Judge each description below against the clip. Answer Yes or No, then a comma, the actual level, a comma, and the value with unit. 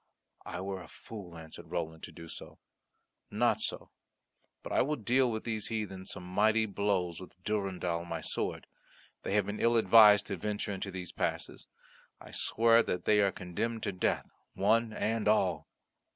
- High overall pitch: No, low, 100 Hz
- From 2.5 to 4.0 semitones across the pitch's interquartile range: Yes, average, 3.4 semitones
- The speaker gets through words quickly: No, average, 165 wpm